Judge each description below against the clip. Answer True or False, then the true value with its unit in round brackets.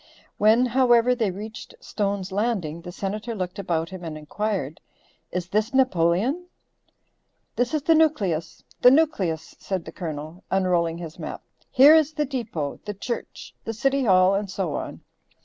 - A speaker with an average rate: True (155 wpm)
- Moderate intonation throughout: False (6.1 semitones)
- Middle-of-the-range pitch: False (200 Hz)